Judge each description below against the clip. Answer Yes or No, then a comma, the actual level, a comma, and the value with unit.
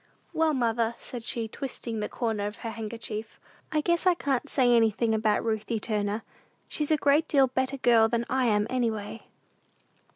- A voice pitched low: No, high, 235 Hz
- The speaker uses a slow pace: No, average, 175 wpm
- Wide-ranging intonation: No, average, 3.1 semitones